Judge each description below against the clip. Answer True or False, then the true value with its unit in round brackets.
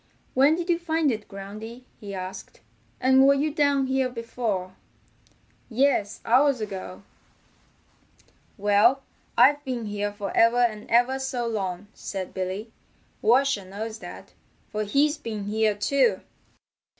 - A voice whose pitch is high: True (230 Hz)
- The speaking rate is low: True (130 wpm)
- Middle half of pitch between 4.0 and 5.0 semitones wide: True (4.6 semitones)